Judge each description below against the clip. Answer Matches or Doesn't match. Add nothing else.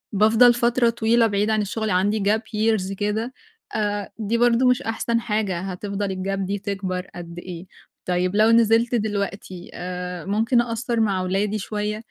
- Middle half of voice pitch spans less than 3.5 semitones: Matches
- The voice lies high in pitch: Matches